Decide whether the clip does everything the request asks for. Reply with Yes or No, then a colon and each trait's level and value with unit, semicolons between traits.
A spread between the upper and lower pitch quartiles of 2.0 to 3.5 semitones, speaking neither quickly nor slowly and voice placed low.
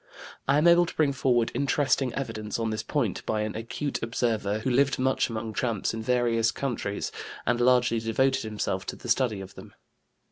Yes: average, 3.2 semitones; average, 185 wpm; low, 120 Hz